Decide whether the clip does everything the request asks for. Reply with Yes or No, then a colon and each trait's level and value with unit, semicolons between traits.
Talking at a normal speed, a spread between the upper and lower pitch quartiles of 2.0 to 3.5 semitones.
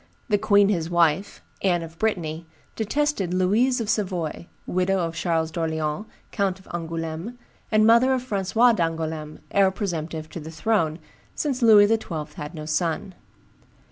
No: average, 145 wpm; average, 4.7 semitones